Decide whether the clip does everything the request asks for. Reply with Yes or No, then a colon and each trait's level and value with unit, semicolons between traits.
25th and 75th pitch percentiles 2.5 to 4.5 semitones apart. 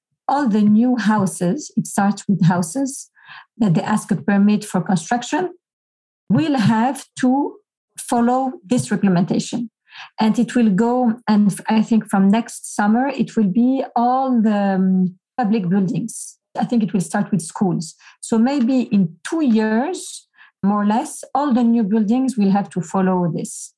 Yes: average, 3.9 semitones